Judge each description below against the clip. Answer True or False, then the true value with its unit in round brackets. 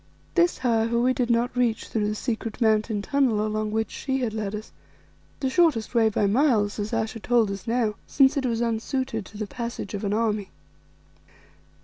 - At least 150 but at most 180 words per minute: False (190 wpm)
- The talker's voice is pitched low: False (225 Hz)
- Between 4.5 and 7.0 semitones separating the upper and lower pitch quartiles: False (2.6 semitones)